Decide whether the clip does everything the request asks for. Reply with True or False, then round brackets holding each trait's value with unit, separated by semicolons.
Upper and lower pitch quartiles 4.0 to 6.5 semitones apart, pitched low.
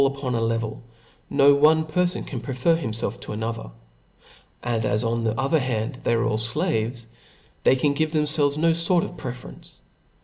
True (5.1 semitones; 130 Hz)